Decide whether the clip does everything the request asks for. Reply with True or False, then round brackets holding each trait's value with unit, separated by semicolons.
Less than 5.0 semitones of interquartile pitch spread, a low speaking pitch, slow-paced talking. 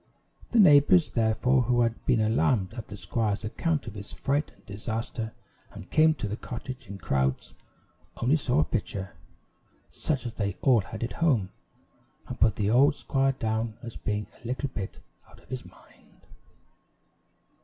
False (4.1 semitones; 115 Hz; 165 wpm)